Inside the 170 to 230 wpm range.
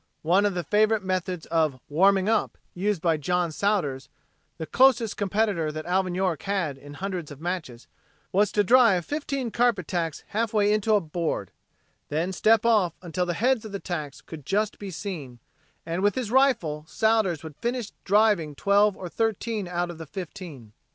Yes: average, 175 wpm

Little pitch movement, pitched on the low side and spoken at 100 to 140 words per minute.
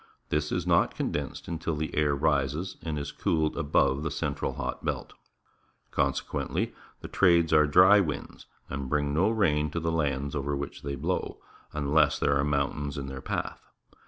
No: narrow, 2.3 semitones; very low, 75 Hz; average, 170 wpm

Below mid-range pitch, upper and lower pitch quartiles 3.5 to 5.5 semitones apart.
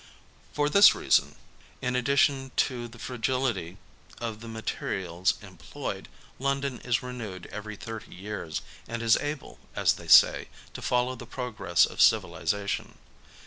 Yes: low, 115 Hz; average, 3.9 semitones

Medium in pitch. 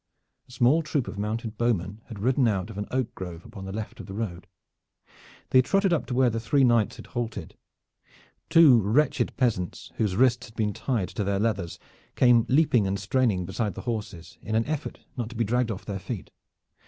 No: low, 115 Hz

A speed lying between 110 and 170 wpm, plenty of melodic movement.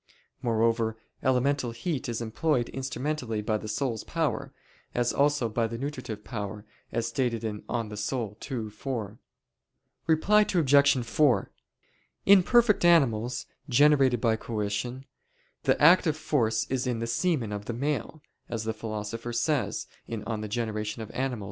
No: slow, 135 wpm; average, 4.1 semitones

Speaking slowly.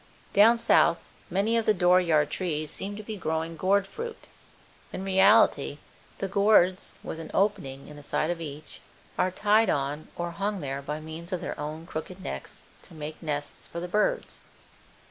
No: average, 180 wpm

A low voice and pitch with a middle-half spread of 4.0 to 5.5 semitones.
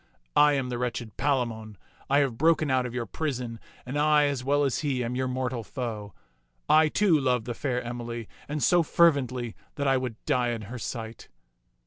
No: low, 125 Hz; average, 3.3 semitones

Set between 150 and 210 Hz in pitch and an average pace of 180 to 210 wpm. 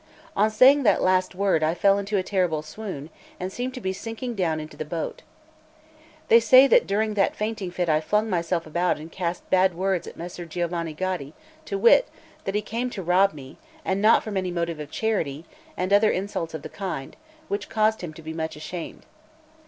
Yes: medium, 185 Hz; fast, 205 wpm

